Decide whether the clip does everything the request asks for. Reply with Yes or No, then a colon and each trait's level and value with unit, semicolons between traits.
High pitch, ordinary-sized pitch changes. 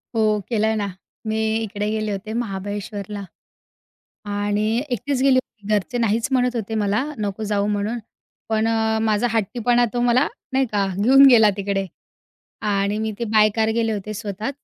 No: high, 215 Hz; narrow, 2.2 semitones